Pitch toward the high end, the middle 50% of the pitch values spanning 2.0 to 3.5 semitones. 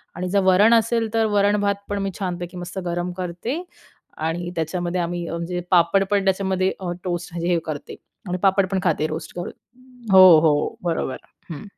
No: medium, 180 Hz; narrow, 2.4 semitones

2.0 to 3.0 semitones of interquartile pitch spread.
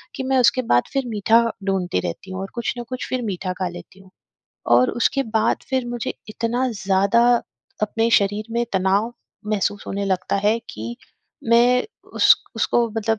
No: average, 3.8 semitones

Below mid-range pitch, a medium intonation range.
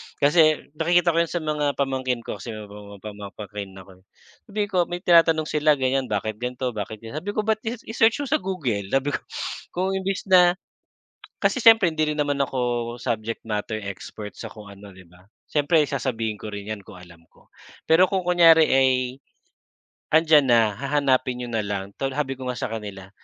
No: low, 130 Hz; wide, 7.0 semitones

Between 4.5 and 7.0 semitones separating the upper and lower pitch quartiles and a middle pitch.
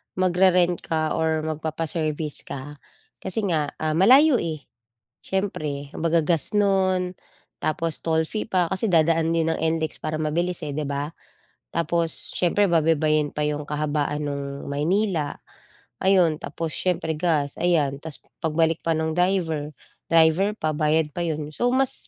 No: average, 2.8 semitones; medium, 160 Hz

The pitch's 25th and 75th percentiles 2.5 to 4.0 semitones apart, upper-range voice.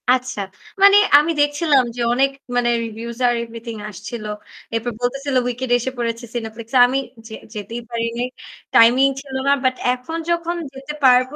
Yes: average, 2.8 semitones; very high, 250 Hz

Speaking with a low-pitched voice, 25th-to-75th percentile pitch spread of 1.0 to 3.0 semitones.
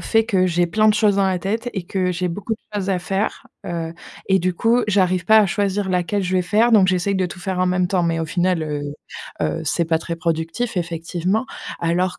No: medium, 185 Hz; average, 2.7 semitones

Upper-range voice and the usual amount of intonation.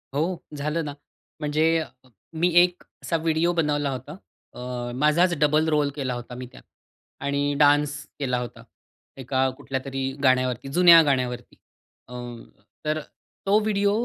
No: medium, 145 Hz; average, 3.6 semitones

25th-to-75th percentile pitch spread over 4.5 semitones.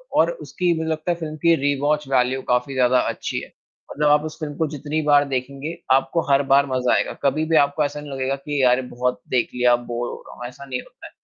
No: average, 2.9 semitones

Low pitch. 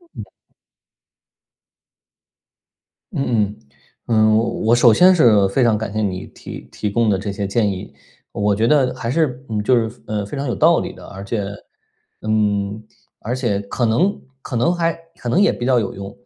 Yes: low, 110 Hz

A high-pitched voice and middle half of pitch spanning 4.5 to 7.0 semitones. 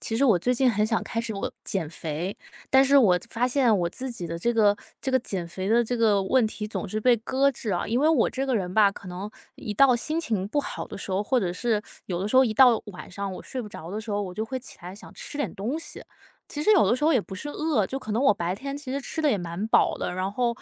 Yes: high, 220 Hz; average, 5.0 semitones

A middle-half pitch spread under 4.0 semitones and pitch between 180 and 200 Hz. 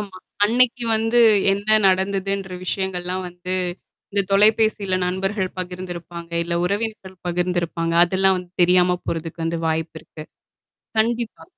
Yes: narrow, 2.4 semitones; medium, 185 Hz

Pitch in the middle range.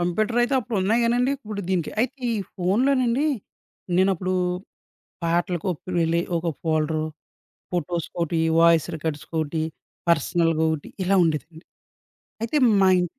Yes: medium, 175 Hz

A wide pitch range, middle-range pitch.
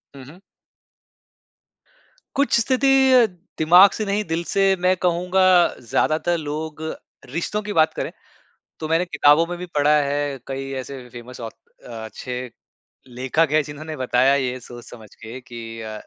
Yes: wide, 5.9 semitones; medium, 150 Hz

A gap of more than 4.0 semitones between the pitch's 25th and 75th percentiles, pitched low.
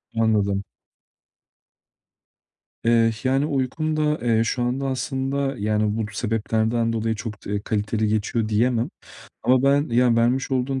No: average, 3.2 semitones; low, 115 Hz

